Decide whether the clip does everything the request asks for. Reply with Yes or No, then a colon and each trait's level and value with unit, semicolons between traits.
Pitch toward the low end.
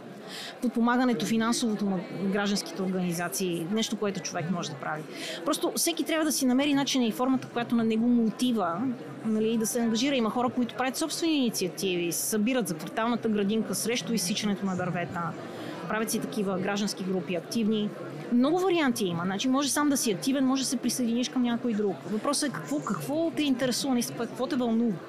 No: high, 230 Hz